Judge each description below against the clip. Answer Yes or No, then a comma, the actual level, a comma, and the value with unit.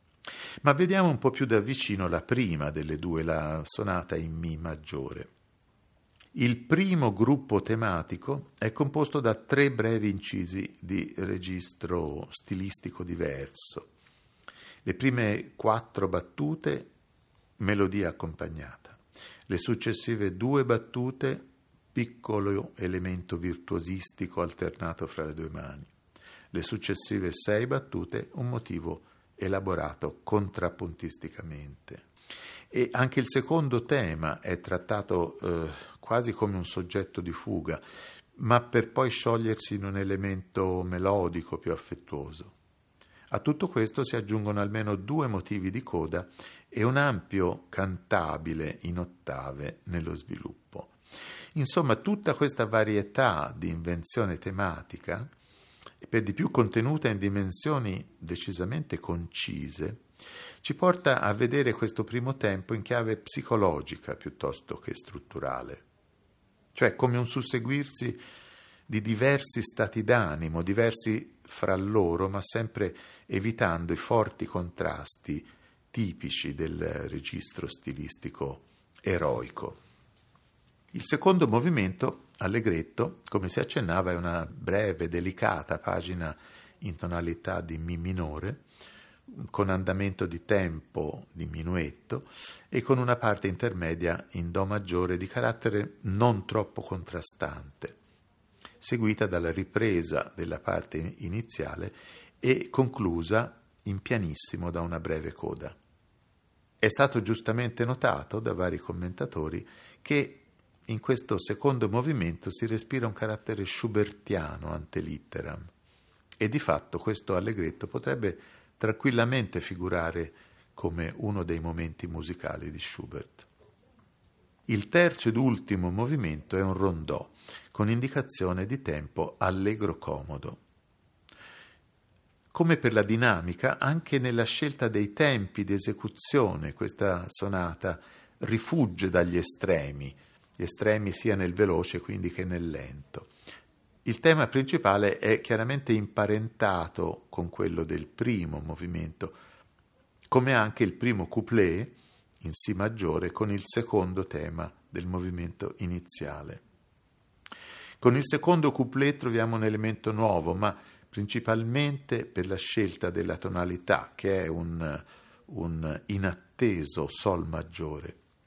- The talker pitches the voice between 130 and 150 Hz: No, low, 100 Hz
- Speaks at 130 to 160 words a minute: No, slow, 115 wpm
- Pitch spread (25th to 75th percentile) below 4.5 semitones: No, average, 5.2 semitones